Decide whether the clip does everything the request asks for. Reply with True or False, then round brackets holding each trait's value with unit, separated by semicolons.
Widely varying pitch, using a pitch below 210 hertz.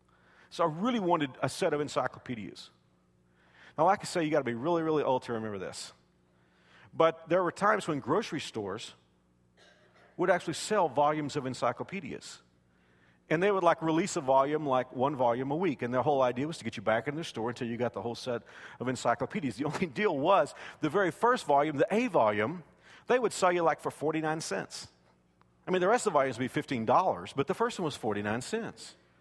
True (7.6 semitones; 135 Hz)